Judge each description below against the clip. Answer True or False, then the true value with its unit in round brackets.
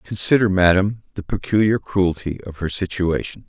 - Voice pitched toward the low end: True (95 Hz)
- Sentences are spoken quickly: False (140 wpm)